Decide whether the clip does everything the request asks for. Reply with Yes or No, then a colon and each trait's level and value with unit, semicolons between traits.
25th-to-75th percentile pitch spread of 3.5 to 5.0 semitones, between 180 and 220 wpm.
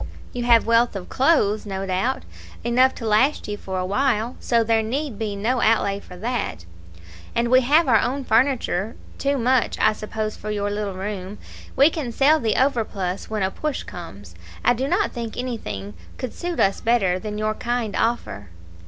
Yes: average, 4.0 semitones; average, 185 wpm